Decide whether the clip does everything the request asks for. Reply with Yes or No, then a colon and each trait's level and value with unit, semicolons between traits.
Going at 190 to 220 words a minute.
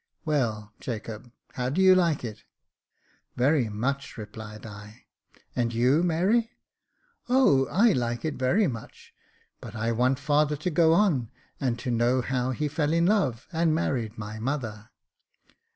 No: average, 165 wpm